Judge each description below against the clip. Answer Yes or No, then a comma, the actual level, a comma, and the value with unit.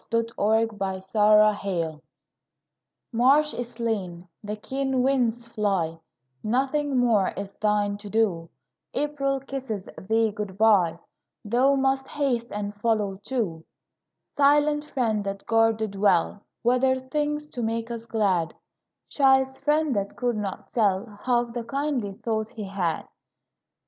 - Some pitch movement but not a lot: Yes, average, 4.4 semitones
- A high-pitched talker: Yes, high, 225 Hz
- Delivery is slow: Yes, slow, 130 wpm